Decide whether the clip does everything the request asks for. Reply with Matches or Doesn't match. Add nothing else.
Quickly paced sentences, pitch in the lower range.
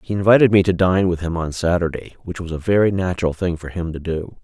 Matches